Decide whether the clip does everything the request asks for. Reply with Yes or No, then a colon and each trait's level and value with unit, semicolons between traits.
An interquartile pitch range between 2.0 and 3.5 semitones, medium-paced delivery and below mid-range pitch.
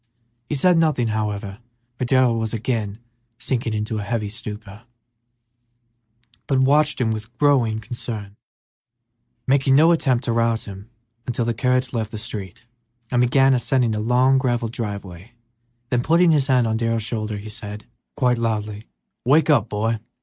Yes: average, 3.2 semitones; average, 155 wpm; low, 115 Hz